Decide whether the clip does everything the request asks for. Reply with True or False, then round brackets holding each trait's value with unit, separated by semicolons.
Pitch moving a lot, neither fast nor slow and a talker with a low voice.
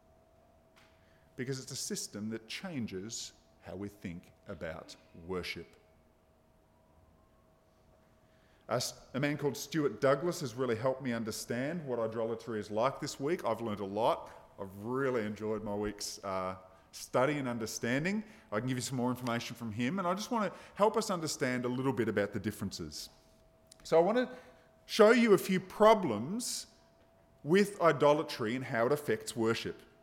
True (6.3 semitones; 160 wpm; 115 Hz)